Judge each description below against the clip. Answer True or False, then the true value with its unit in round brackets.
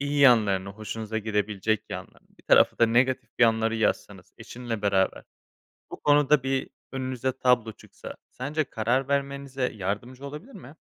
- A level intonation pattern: False (3.7 semitones)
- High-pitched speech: False (120 Hz)